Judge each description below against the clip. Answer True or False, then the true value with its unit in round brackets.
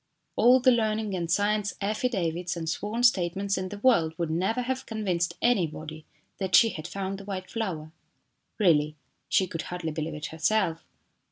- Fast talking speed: False (165 wpm)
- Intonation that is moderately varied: True (4.6 semitones)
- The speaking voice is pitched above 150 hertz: True (190 Hz)